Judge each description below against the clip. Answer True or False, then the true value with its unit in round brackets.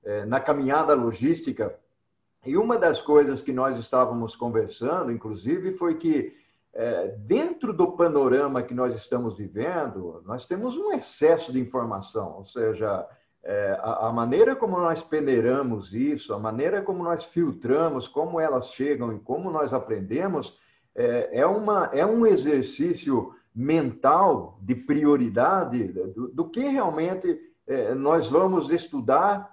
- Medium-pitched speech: True (165 Hz)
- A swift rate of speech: False (125 wpm)